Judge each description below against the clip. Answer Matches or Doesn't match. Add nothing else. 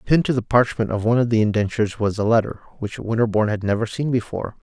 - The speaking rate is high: Matches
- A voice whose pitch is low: Matches